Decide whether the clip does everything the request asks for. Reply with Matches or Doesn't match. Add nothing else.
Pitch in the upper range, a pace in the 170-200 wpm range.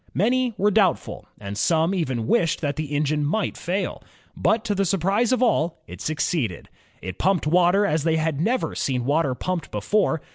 Doesn't match